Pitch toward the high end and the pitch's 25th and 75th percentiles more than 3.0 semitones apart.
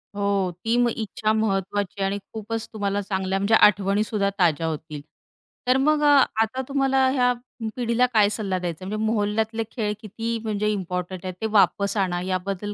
No: high, 205 Hz; average, 2.7 semitones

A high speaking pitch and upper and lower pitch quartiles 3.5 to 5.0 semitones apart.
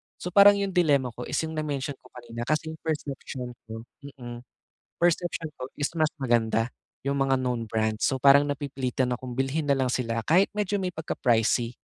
No: low, 135 Hz; average, 4.5 semitones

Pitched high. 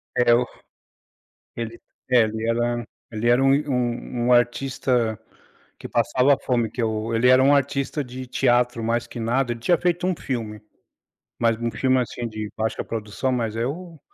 No: low, 120 Hz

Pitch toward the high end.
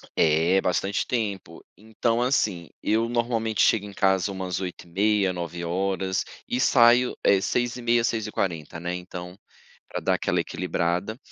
No: low, 100 Hz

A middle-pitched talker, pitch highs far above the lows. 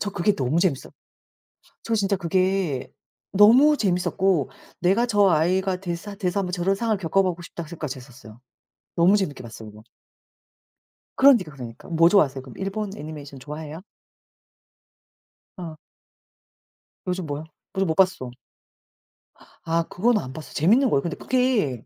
No: medium, 180 Hz; average, 4.7 semitones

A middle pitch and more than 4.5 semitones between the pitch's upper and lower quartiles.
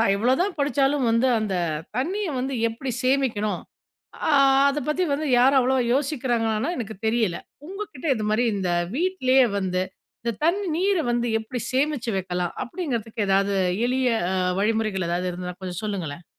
No: high, 240 Hz; average, 5.2 semitones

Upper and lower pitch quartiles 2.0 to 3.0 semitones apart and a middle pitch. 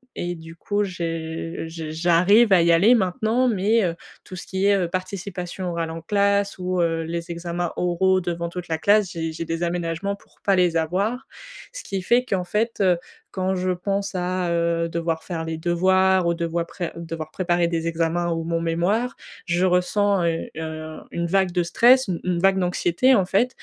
Yes: narrow, 2.5 semitones; medium, 175 Hz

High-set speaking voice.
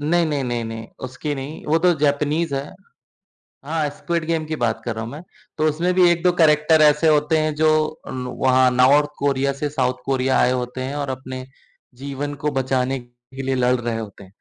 No: medium, 140 Hz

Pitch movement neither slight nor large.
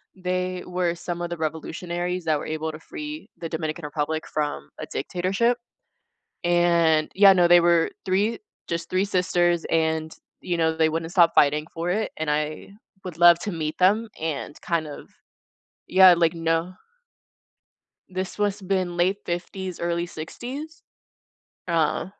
No: narrow, 2.3 semitones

